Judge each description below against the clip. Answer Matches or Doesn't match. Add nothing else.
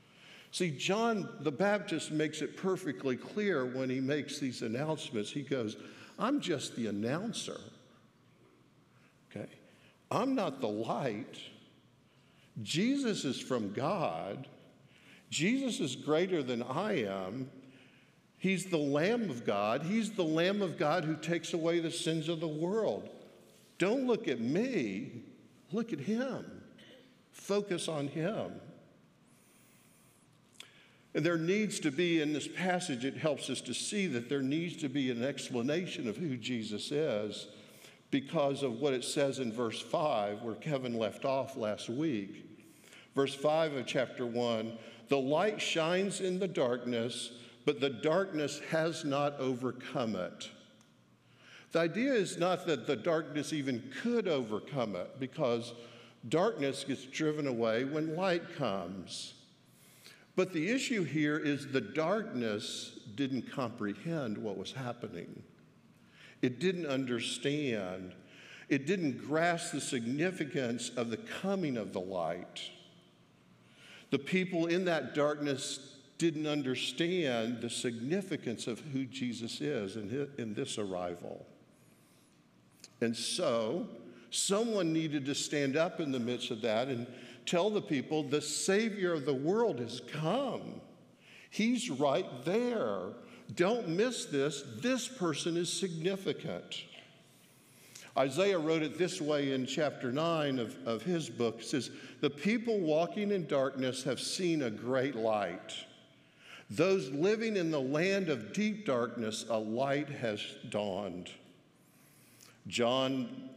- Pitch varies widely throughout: Matches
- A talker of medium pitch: Matches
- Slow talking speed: Matches